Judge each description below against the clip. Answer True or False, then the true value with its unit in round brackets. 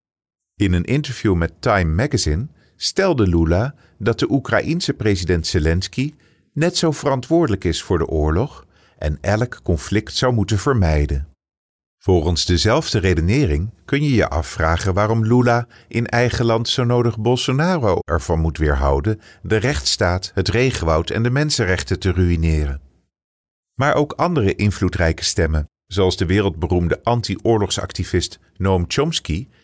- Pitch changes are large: True (5.7 semitones)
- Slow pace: True (130 wpm)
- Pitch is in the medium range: False (100 Hz)